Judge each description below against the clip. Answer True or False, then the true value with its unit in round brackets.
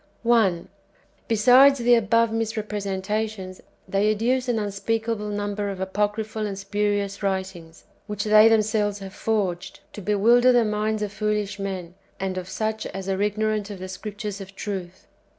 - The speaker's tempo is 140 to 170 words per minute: True (150 wpm)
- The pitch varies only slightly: True (2.0 semitones)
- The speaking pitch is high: True (210 Hz)